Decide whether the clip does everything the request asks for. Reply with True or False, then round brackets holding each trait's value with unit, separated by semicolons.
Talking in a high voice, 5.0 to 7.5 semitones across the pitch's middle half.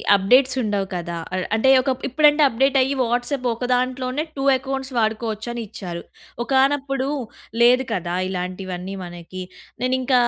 True (245 Hz; 5.4 semitones)